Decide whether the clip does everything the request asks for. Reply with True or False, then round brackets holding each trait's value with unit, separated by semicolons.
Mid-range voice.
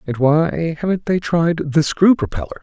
True (155 Hz)